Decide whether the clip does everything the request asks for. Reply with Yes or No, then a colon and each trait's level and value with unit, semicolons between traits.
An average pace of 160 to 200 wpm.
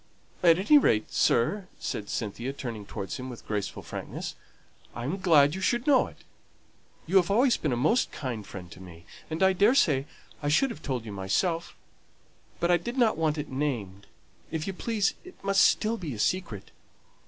Yes: average, 190 wpm